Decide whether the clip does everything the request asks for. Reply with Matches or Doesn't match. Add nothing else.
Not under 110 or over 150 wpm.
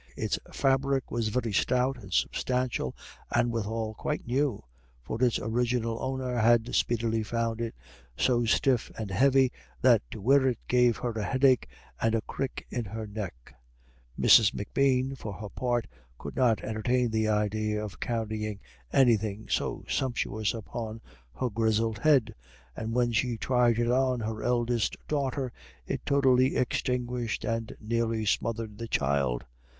Matches